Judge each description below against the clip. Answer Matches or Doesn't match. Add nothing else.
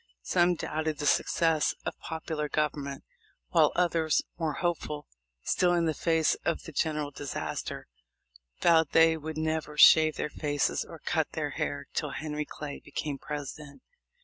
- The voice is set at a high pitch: Doesn't match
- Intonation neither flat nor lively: Doesn't match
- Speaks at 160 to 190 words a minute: Doesn't match